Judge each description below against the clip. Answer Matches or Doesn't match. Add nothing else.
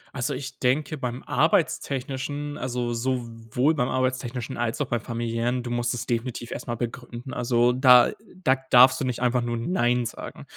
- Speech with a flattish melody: Matches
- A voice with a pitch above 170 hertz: Doesn't match